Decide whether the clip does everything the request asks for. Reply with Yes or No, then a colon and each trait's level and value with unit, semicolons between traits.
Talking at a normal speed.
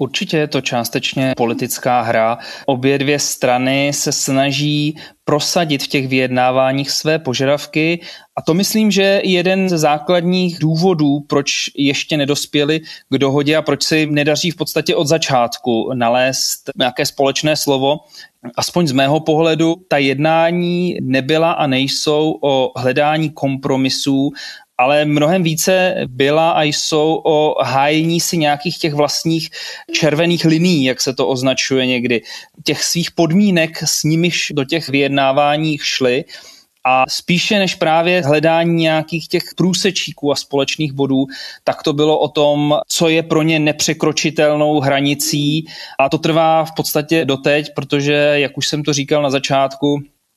Yes: average, 140 wpm